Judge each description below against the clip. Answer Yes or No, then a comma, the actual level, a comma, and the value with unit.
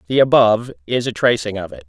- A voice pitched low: Yes, low, 110 Hz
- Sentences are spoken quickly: Yes, fast, 225 wpm